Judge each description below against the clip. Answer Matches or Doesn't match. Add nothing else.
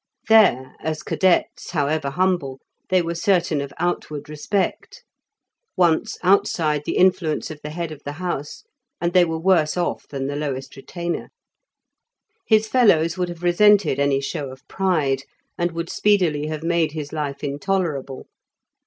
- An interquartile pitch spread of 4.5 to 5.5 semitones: Doesn't match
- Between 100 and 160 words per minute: Matches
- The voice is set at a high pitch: Doesn't match